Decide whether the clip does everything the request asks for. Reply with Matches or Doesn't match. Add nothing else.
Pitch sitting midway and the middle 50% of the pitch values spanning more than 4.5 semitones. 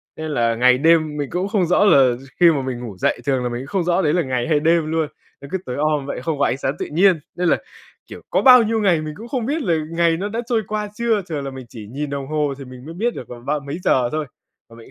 Matches